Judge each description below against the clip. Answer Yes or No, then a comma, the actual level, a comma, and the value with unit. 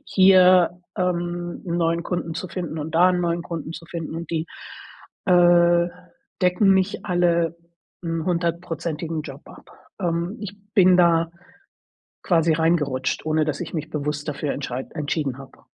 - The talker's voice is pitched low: No, medium, 170 Hz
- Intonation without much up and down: Yes, narrow, 1.9 semitones